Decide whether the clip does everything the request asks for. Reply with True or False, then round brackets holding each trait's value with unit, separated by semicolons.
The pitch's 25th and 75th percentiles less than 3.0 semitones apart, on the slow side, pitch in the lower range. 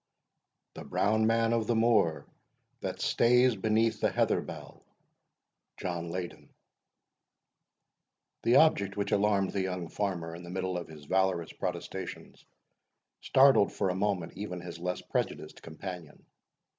False (3.9 semitones; 130 wpm; 95 Hz)